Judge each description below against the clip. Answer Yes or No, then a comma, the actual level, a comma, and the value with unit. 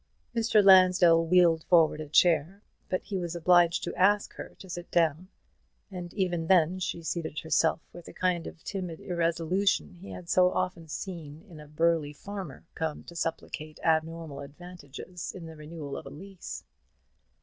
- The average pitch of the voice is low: No, medium, 170 Hz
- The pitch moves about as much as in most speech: No, narrow, 2.3 semitones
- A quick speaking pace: No, average, 165 wpm